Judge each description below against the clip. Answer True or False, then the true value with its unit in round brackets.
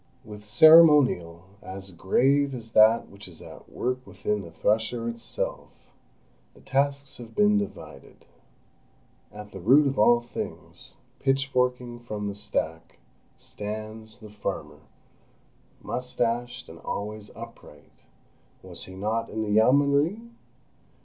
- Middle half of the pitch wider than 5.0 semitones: False (3.8 semitones)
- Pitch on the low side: True (115 Hz)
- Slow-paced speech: True (115 wpm)